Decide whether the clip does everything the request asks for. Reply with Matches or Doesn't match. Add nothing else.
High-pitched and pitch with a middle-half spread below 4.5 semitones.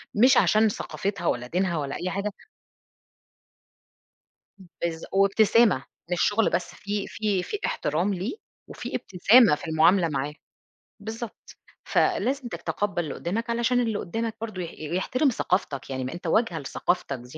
Doesn't match